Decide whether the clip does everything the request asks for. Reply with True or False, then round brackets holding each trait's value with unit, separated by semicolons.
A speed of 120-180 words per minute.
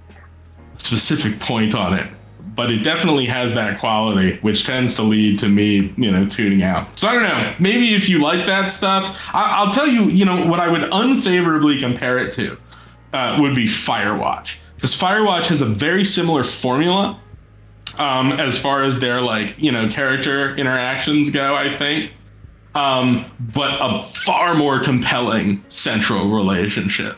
True (165 wpm)